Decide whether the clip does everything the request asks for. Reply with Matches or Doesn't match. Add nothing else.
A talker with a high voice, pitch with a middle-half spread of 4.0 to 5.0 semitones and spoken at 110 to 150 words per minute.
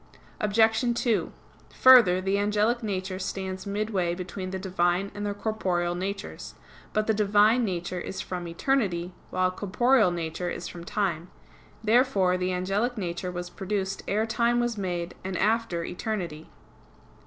Doesn't match